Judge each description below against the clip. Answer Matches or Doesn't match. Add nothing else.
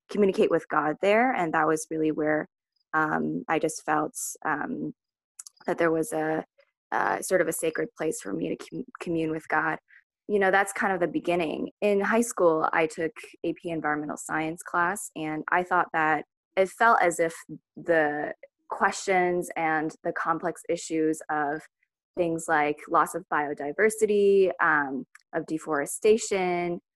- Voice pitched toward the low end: Doesn't match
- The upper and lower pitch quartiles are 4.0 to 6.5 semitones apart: Doesn't match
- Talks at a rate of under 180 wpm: Matches